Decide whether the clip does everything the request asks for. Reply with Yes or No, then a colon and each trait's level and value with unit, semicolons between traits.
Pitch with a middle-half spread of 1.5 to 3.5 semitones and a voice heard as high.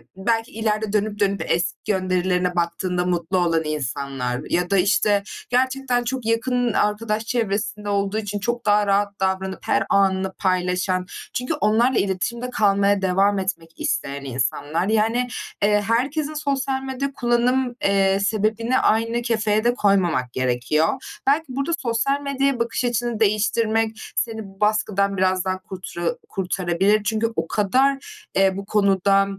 No: average, 3.9 semitones; high, 210 Hz